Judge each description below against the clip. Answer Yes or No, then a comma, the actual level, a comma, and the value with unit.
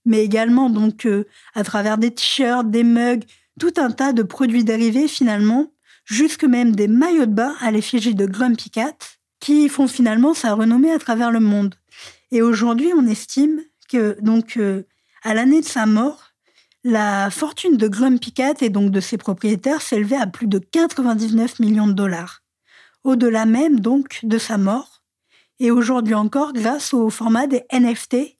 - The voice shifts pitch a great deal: No, average, 3.4 semitones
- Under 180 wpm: Yes, average, 170 wpm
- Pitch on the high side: Yes, high, 235 Hz